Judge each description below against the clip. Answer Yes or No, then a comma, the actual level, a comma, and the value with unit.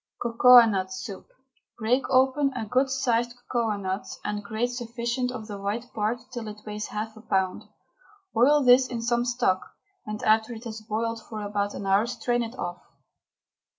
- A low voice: No, high, 230 Hz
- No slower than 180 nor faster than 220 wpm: No, average, 165 wpm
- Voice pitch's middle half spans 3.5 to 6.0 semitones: No, narrow, 2.6 semitones